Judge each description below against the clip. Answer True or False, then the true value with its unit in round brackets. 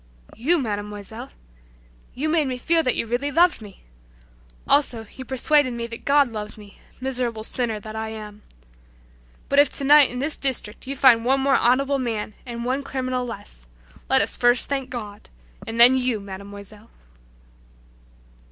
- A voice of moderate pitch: False (245 Hz)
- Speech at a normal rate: True (160 wpm)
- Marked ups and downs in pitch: False (3.7 semitones)